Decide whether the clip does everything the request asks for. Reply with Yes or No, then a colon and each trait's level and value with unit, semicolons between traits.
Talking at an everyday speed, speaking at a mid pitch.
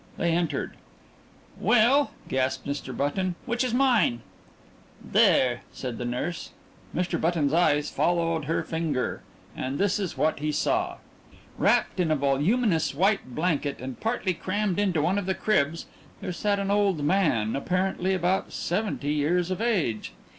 Yes: average, 150 wpm; medium, 170 Hz